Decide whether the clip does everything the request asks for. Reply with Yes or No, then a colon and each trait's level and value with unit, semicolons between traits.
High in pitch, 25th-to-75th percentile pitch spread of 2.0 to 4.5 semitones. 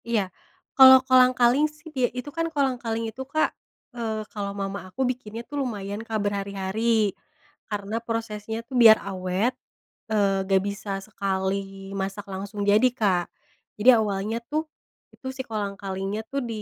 Yes: high, 215 Hz; average, 3.7 semitones